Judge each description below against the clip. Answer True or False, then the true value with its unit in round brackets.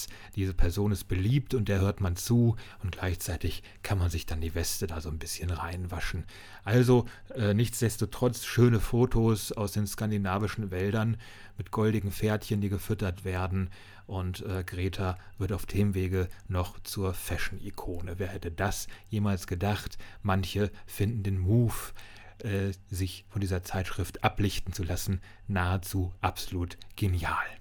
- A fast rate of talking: False (145 wpm)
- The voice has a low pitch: True (100 Hz)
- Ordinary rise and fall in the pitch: False (2.1 semitones)